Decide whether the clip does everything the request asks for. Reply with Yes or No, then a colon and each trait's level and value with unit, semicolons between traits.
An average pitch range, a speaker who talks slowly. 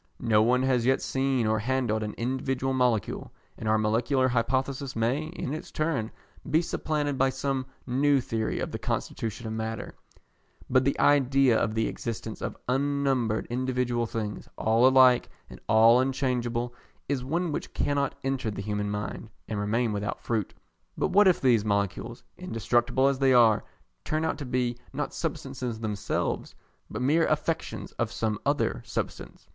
No: average, 3.3 semitones; average, 160 wpm